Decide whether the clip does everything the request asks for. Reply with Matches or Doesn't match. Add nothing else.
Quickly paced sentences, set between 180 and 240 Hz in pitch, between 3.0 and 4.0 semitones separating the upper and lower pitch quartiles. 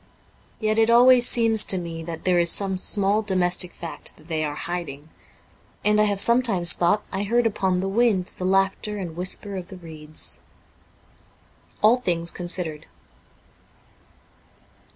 Doesn't match